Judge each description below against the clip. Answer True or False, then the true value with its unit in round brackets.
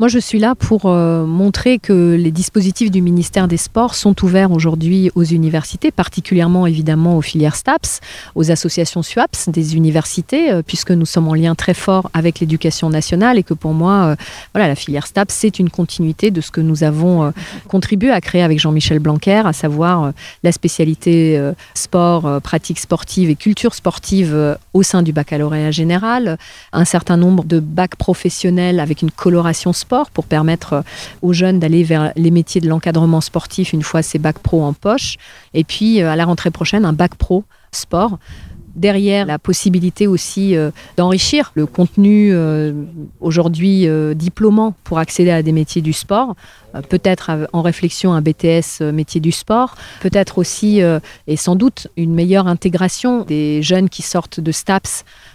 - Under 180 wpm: True (170 wpm)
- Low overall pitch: False (170 Hz)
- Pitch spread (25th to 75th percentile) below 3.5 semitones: True (2.8 semitones)